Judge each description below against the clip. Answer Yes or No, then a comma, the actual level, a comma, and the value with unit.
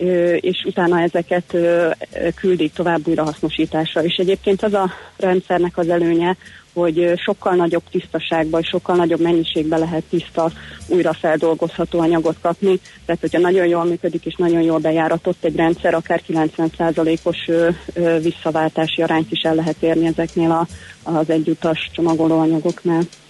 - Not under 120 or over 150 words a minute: Yes, average, 130 wpm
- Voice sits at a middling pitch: Yes, medium, 170 Hz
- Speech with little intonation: Yes, narrow, 1.2 semitones